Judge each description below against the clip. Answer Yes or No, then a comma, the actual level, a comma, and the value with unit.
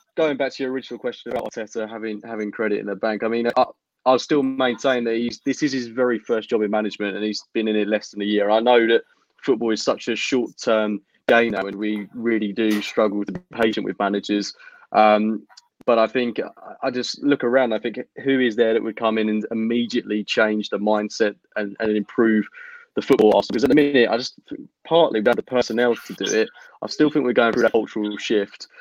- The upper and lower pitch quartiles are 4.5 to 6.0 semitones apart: No, average, 3.1 semitones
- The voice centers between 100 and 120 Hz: Yes, low, 115 Hz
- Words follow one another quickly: Yes, fast, 225 wpm